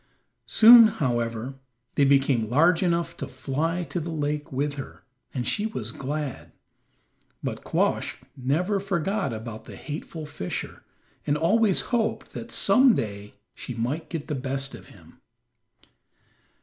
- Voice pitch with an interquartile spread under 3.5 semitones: No, average, 4.9 semitones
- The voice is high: No, medium, 145 Hz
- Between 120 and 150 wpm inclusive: Yes, slow, 135 wpm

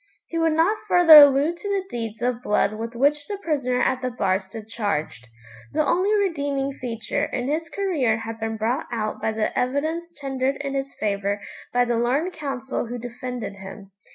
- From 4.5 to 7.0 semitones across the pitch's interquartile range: Yes, average, 5.2 semitones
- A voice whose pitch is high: Yes, very high, 255 Hz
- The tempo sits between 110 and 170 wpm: No, average, 185 wpm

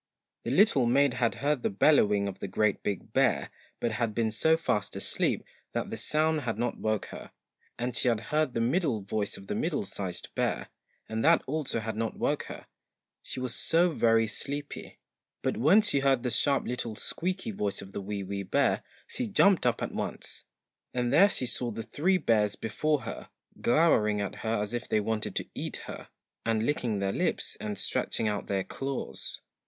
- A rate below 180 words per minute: No, average, 195 wpm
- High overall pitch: No, low, 120 Hz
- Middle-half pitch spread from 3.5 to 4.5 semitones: No, average, 5.3 semitones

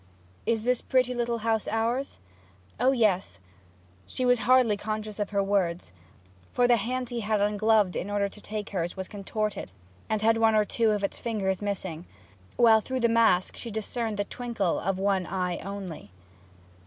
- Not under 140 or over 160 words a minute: No, average, 175 wpm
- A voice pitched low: No, high, 215 Hz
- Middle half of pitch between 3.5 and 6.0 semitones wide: No, average, 2.8 semitones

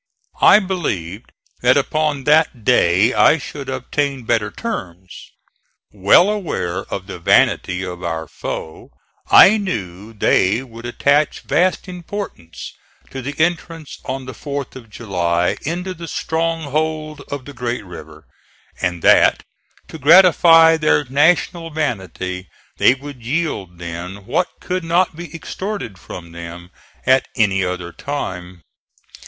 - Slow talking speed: Yes, slow, 130 wpm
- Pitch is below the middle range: Yes, low, 130 Hz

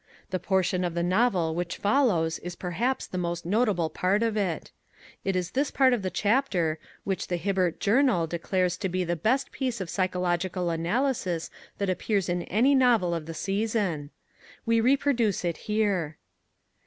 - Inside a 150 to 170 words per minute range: Yes, average, 165 wpm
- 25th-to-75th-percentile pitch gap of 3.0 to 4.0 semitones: No, average, 4.5 semitones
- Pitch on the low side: No, medium, 185 Hz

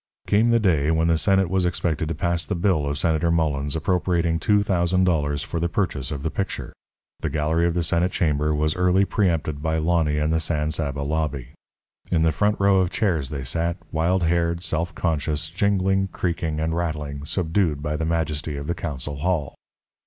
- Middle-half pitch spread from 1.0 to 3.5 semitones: Yes, average, 2.8 semitones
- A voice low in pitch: Yes, very low, 80 Hz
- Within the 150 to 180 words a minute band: No, average, 195 wpm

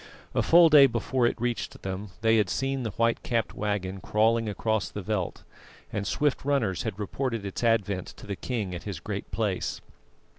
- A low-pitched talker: Yes, low, 110 Hz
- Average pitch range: Yes, average, 3.4 semitones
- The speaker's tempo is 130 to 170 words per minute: No, average, 185 wpm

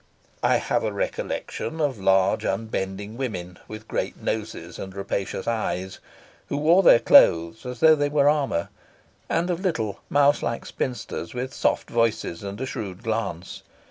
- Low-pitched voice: Yes, low, 115 Hz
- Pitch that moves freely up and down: Yes, wide, 6.9 semitones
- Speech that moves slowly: No, average, 155 wpm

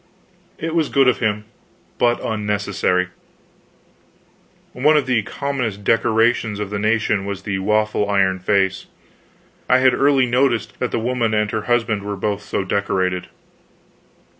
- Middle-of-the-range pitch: No, low, 110 Hz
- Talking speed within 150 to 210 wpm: No, average, 140 wpm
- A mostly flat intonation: No, average, 3.3 semitones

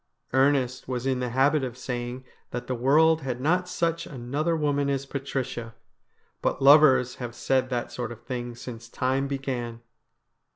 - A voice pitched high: No, low, 130 Hz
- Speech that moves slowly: No, average, 160 wpm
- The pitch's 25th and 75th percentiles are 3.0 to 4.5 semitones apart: No, narrow, 2.4 semitones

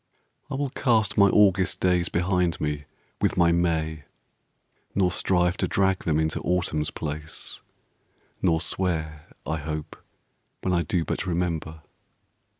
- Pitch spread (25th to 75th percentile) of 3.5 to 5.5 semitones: No, average, 2.8 semitones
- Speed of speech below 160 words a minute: Yes, slow, 135 wpm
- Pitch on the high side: No, very low, 85 Hz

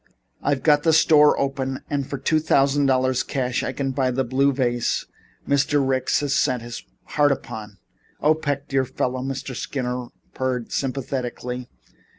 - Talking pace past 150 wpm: Yes, average, 160 wpm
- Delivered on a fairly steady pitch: Yes, narrow, 2.0 semitones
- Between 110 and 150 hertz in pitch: Yes, low, 135 Hz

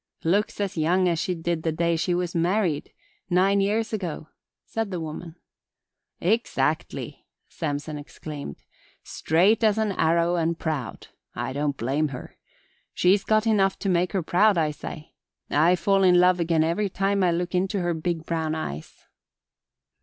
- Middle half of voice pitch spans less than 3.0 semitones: No, average, 3.4 semitones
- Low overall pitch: No, medium, 175 Hz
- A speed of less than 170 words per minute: Yes, average, 160 wpm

